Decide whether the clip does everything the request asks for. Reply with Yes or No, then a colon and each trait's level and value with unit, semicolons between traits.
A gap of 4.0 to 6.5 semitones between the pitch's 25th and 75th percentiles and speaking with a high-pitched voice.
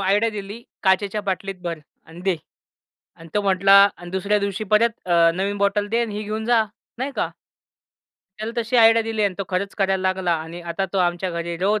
No: narrow, 2.6 semitones; high, 195 Hz